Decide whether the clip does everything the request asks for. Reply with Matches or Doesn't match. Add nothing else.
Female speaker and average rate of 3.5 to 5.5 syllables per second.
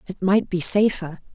Matches